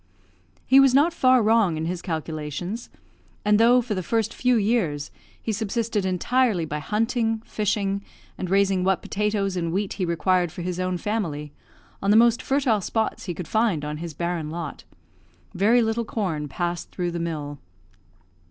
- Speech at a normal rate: Yes, average, 170 wpm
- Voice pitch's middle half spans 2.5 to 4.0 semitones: No, average, 4.7 semitones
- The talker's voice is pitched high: Yes, high, 195 Hz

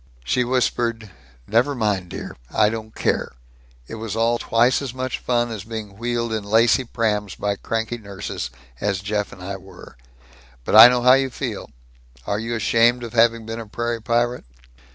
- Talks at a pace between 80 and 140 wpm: No, average, 175 wpm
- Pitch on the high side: No, low, 115 Hz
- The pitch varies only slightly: Yes, narrow, 2.3 semitones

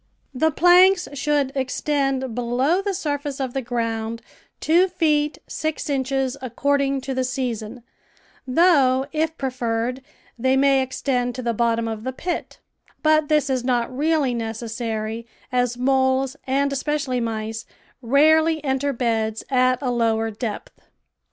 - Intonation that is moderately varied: Yes, average, 3.4 semitones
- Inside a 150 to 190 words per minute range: No, average, 140 wpm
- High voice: Yes, very high, 260 Hz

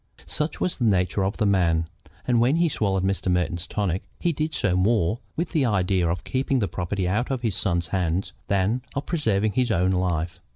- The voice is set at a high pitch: No, low, 100 Hz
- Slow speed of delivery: No, fast, 205 wpm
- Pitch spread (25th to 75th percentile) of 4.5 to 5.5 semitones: Yes, average, 5.1 semitones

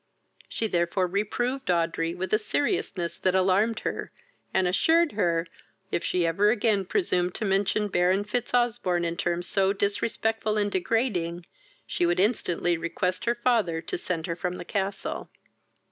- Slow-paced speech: No, average, 150 wpm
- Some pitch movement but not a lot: Yes, average, 3.6 semitones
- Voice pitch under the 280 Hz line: Yes, high, 190 Hz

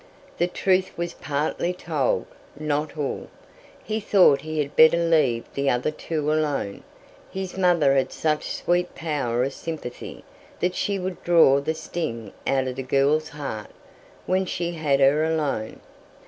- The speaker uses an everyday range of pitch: Yes, average, 3.8 semitones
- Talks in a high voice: No, medium, 155 Hz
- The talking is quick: No, average, 150 wpm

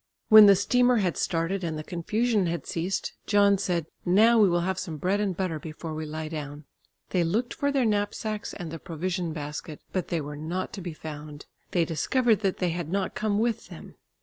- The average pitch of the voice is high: No, medium, 180 Hz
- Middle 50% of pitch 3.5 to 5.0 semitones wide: Yes, average, 4.3 semitones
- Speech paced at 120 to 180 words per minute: No, fast, 205 wpm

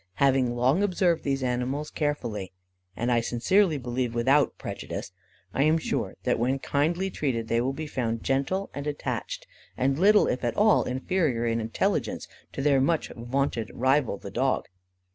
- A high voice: No, low, 135 Hz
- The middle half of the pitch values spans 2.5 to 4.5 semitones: Yes, average, 3.8 semitones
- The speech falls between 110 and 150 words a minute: No, average, 160 wpm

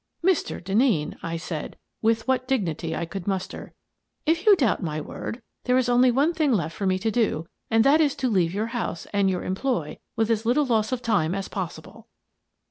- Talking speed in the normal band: No, fast, 215 wpm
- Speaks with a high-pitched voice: Yes, high, 225 Hz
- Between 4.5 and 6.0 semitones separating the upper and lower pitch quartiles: Yes, wide, 5.5 semitones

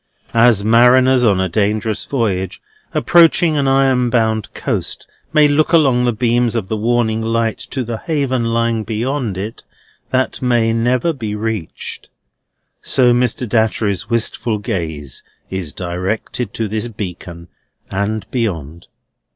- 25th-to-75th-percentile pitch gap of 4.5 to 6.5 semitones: No, average, 3.1 semitones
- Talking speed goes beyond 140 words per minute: No, slow, 135 wpm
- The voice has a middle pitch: No, low, 115 Hz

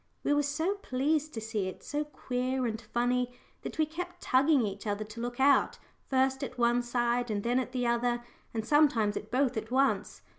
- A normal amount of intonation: Yes, average, 3.1 semitones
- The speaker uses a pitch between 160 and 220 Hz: No, very high, 250 Hz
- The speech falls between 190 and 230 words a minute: Yes, average, 200 wpm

